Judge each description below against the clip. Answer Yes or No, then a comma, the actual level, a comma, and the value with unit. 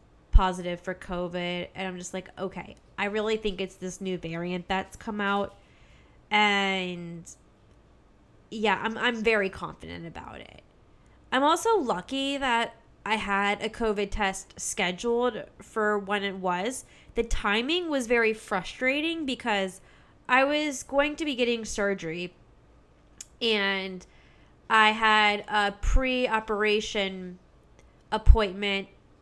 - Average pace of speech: No, slow, 125 wpm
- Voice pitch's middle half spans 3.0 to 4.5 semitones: Yes, average, 3.6 semitones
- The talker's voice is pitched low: No, high, 205 Hz